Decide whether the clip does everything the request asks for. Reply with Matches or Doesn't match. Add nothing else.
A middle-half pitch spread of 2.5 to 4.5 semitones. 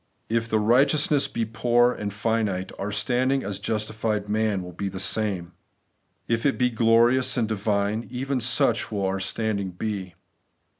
Matches